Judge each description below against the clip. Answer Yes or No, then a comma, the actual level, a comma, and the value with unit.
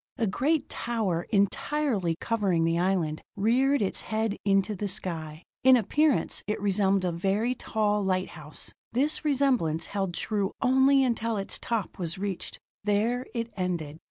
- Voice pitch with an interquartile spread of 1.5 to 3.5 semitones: No, average, 4.5 semitones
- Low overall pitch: No, high, 205 Hz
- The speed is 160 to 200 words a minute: No, average, 145 wpm